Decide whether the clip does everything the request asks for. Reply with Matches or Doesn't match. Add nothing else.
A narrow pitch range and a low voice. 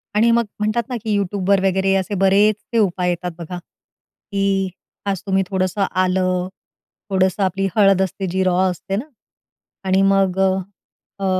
Doesn't match